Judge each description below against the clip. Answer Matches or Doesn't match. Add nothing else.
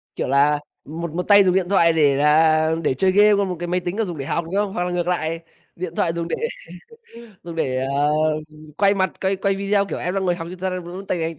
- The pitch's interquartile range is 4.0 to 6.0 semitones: Doesn't match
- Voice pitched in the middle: Matches